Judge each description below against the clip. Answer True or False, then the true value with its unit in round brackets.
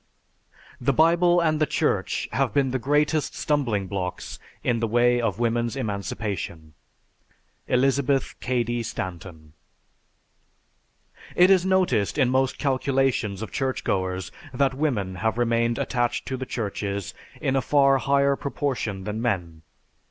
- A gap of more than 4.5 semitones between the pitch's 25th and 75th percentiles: True (5.0 semitones)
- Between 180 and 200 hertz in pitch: False (120 Hz)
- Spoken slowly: True (130 wpm)